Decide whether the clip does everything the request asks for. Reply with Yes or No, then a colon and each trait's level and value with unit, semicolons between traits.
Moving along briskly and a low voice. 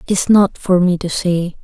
No: fast, 255 wpm; medium, 185 Hz